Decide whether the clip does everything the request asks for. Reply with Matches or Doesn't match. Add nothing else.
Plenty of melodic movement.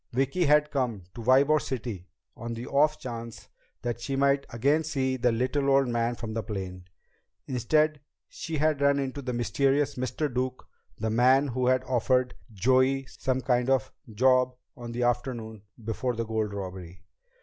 Doesn't match